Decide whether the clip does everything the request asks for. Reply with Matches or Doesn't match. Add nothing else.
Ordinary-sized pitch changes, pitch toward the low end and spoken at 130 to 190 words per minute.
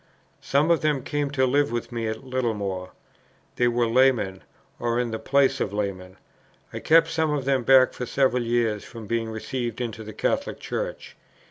Matches